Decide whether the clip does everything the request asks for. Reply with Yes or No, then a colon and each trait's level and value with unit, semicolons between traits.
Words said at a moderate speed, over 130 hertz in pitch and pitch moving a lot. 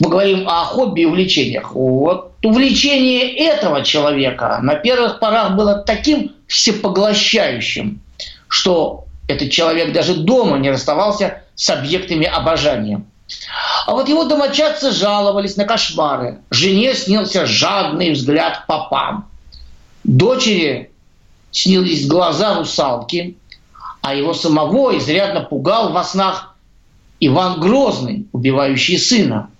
No: slow, 105 wpm; medium, 185 Hz; wide, 6.4 semitones